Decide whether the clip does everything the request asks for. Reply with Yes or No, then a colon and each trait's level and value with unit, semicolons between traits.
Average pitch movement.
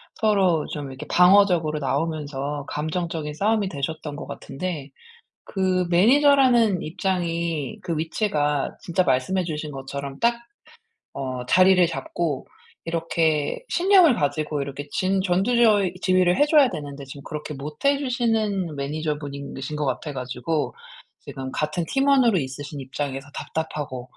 Yes: average, 4.9 semitones